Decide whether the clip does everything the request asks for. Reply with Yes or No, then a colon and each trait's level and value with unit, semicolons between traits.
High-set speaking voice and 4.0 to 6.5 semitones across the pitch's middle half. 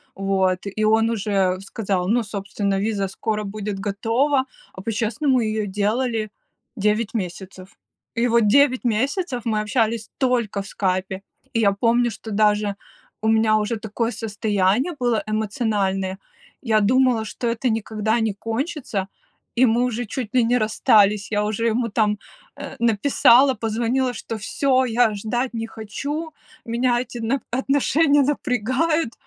No: high, 220 Hz; average, 2.9 semitones